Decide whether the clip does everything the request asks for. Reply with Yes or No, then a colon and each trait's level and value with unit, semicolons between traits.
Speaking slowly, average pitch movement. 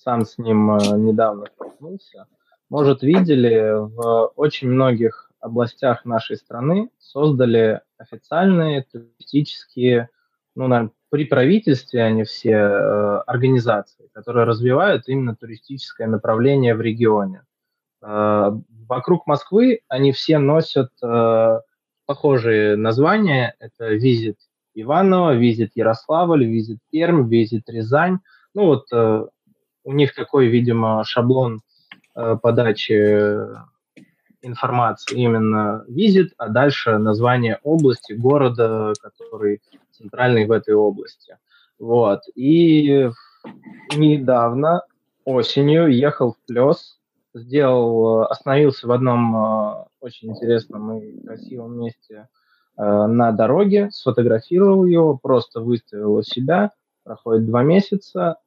Yes: slow, 105 wpm; average, 4.4 semitones